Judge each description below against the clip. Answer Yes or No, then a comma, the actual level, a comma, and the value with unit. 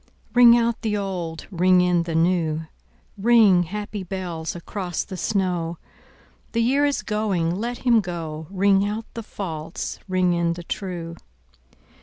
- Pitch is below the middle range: No, medium, 185 Hz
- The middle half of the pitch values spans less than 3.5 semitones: No, average, 3.8 semitones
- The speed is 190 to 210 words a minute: No, average, 145 wpm